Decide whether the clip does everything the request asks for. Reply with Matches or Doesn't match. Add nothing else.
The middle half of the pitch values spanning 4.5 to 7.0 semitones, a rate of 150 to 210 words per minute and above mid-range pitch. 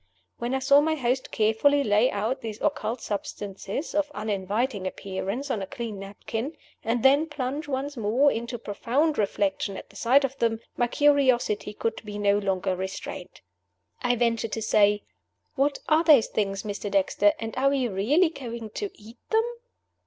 Matches